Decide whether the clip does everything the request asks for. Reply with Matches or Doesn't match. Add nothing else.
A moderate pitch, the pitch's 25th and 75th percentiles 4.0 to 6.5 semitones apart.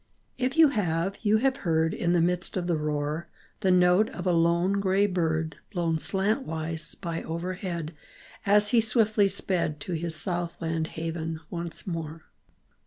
Doesn't match